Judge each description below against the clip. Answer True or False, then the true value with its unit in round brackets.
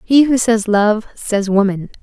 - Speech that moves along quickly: False (180 wpm)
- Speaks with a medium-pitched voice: False (220 Hz)